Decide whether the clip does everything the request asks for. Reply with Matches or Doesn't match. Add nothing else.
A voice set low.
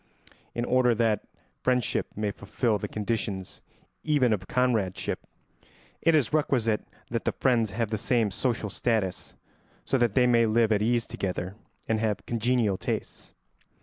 Matches